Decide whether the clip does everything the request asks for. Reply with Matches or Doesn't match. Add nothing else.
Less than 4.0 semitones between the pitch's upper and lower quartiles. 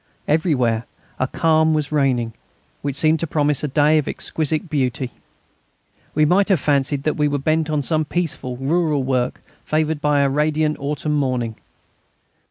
Matches